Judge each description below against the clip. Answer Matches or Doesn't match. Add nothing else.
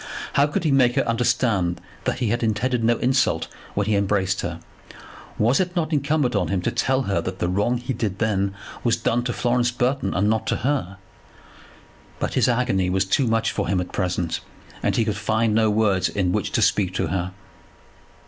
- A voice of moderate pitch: Doesn't match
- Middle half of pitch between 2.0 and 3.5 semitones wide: Doesn't match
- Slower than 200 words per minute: Doesn't match